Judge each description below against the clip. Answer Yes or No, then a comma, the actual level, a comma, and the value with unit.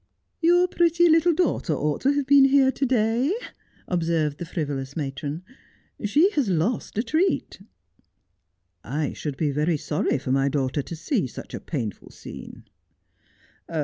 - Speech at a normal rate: Yes, average, 160 wpm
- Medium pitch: Yes, medium, 170 Hz